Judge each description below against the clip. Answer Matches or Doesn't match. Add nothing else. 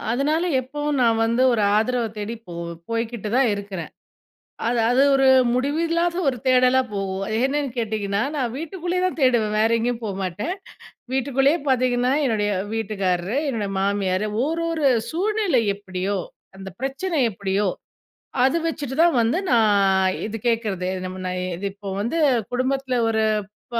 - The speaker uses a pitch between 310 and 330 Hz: Doesn't match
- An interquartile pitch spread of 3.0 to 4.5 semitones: Doesn't match